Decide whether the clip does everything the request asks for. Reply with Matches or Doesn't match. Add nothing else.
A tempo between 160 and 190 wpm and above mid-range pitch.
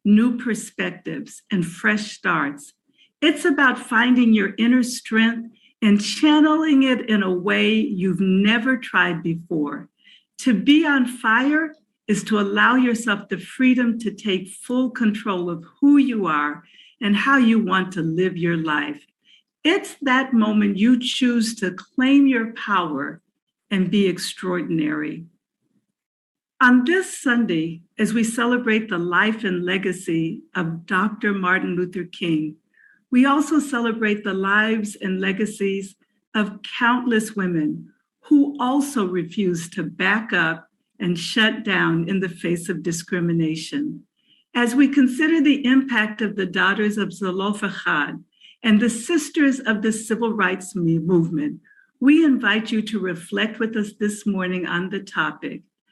Doesn't match